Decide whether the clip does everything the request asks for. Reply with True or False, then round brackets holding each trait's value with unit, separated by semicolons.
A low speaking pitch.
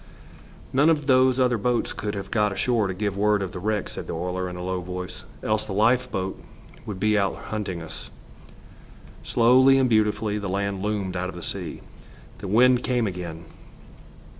True (105 Hz)